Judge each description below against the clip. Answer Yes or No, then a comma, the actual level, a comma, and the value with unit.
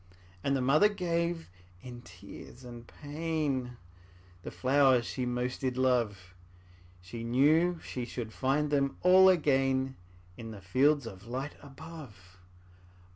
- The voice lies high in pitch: No, low, 130 Hz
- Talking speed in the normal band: No, slow, 130 wpm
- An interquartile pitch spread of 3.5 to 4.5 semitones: Yes, average, 4.1 semitones